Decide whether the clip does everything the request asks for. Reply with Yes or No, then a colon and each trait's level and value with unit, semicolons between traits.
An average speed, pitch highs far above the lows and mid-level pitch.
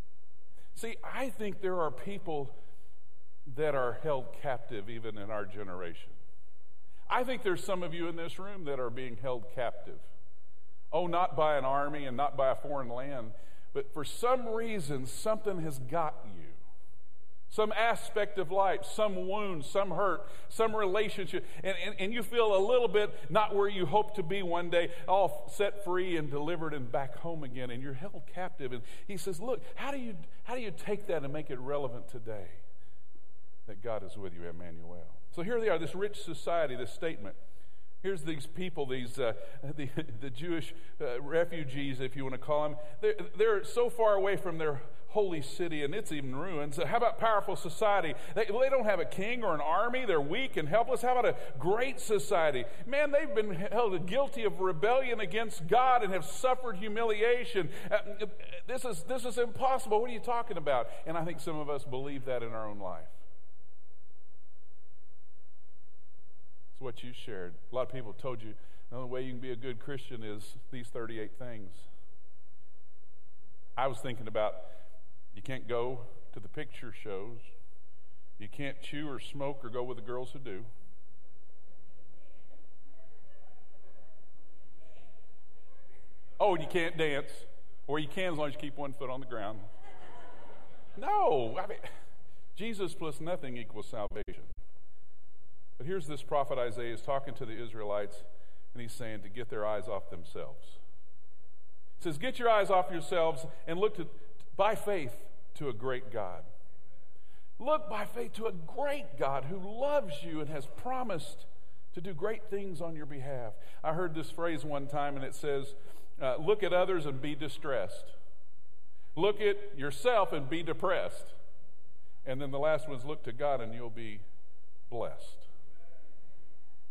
Yes: average, 175 wpm; wide, 9.0 semitones; medium, 145 Hz